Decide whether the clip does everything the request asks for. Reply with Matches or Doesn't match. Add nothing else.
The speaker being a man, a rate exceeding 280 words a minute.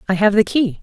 Doesn't match